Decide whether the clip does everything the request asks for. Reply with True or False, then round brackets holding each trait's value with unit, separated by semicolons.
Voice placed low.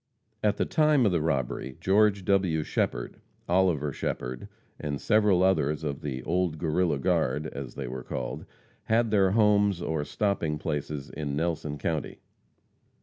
True (80 Hz)